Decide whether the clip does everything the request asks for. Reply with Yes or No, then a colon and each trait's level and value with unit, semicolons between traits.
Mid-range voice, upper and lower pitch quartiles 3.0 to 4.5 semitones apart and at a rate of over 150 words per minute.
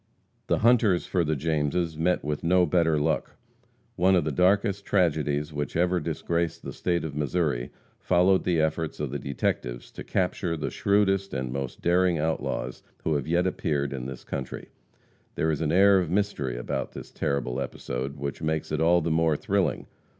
No: very low, 80 Hz; average, 3.8 semitones; average, 180 wpm